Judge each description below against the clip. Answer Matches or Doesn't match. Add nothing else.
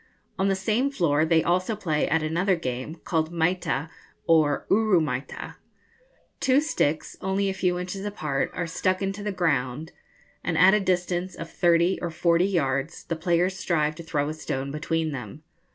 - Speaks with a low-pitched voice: Doesn't match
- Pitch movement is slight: Doesn't match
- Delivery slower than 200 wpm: Matches